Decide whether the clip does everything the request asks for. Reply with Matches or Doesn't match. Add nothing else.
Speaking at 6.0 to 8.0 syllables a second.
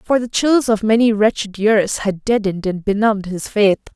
Doesn't match